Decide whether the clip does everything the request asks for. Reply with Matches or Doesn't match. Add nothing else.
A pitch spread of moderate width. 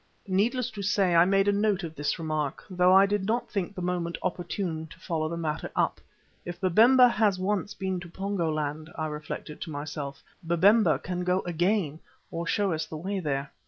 Matches